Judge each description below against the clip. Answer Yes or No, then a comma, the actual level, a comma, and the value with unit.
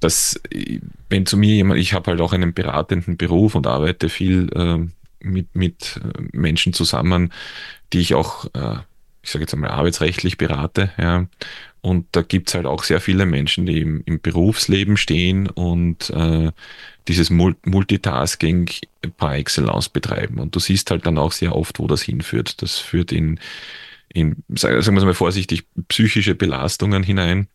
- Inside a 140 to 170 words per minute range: Yes, average, 165 wpm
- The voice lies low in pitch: Yes, very low, 90 Hz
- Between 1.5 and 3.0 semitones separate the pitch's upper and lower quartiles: Yes, narrow, 2.5 semitones